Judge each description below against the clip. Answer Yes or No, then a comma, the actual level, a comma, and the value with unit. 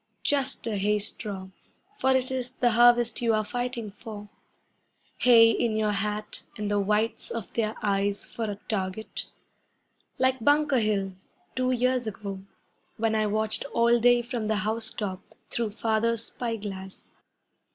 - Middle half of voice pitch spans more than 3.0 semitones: No, narrow, 2.5 semitones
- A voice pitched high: Yes, high, 220 Hz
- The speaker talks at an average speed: Yes, average, 150 wpm